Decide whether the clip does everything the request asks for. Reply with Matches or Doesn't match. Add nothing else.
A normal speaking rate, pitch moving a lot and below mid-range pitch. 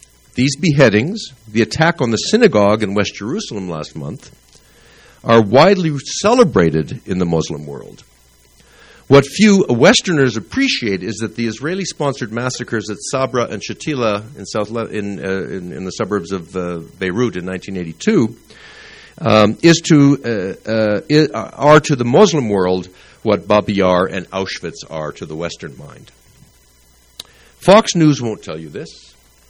Matches